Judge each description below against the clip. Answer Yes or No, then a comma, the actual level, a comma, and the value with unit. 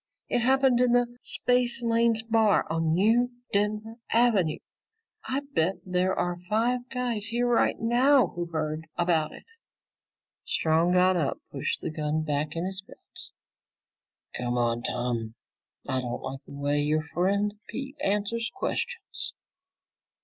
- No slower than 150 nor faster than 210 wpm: No, slow, 135 wpm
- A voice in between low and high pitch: No, high, 195 Hz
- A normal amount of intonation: No, wide, 7.2 semitones